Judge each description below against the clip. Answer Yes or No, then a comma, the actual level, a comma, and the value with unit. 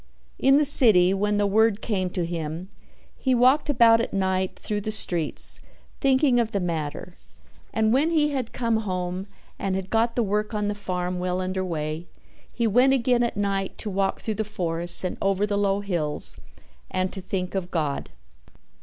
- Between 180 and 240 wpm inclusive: Yes, average, 185 wpm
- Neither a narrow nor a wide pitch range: Yes, average, 3.9 semitones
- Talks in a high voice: Yes, high, 200 Hz